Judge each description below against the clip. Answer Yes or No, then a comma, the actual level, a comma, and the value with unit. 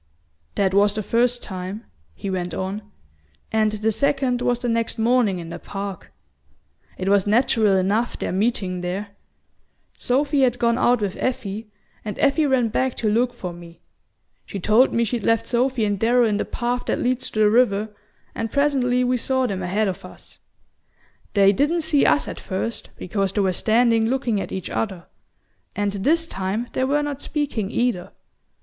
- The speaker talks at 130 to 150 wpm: No, average, 180 wpm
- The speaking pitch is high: Yes, high, 225 Hz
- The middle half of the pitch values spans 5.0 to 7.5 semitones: No, average, 4.0 semitones